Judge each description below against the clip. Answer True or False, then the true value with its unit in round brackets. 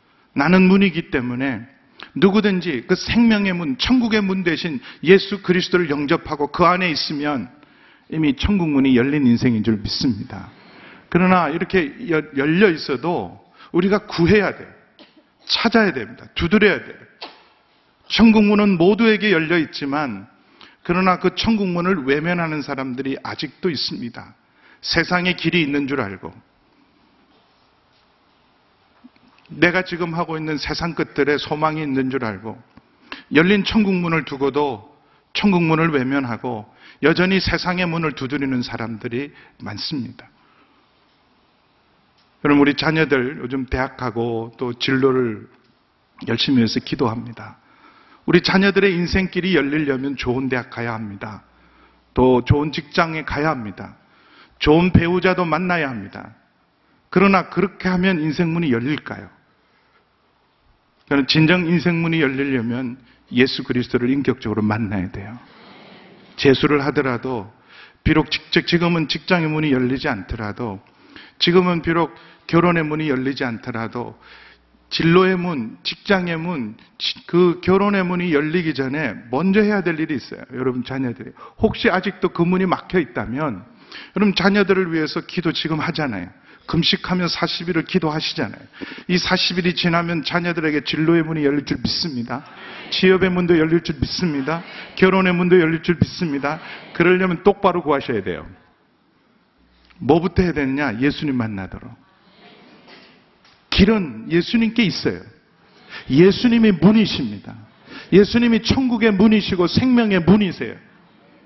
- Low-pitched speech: False (165 Hz)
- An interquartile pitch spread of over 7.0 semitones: False (5.5 semitones)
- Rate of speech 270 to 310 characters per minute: True (295 characters per minute)